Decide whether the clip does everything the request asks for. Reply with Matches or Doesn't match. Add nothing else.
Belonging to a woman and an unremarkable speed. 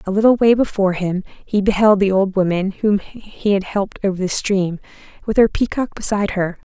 Matches